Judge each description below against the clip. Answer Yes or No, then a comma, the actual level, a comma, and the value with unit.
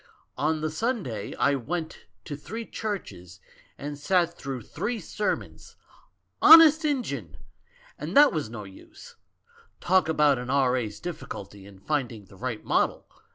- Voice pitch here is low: No, medium, 150 Hz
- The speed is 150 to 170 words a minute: No, slow, 135 wpm